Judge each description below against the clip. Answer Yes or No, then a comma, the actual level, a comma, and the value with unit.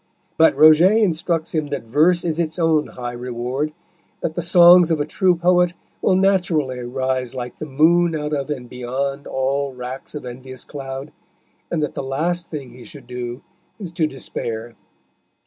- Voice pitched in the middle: Yes, medium, 150 Hz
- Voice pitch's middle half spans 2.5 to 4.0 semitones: No, average, 4.7 semitones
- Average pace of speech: Yes, average, 170 wpm